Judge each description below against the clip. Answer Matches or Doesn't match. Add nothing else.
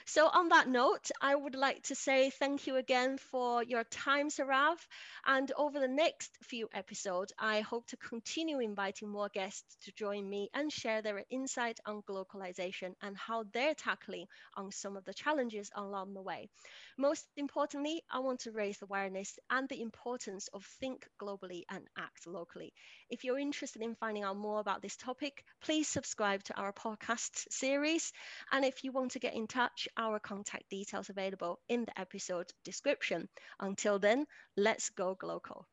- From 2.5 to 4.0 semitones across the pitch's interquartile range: Doesn't match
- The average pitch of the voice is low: Doesn't match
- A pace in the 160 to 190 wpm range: Matches